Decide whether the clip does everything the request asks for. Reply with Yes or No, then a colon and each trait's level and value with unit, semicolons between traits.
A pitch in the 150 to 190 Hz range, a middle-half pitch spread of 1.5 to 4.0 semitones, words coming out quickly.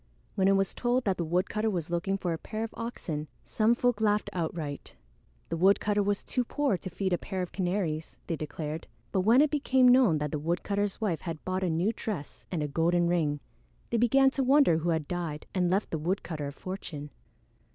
No: medium, 185 Hz; average, 4.8 semitones; fast, 210 wpm